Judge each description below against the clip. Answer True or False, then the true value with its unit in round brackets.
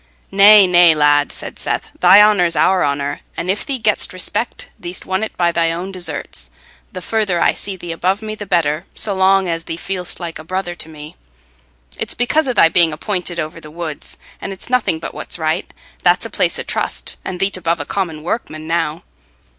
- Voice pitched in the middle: True (175 Hz)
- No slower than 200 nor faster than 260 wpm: True (205 wpm)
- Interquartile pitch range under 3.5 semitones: True (2.9 semitones)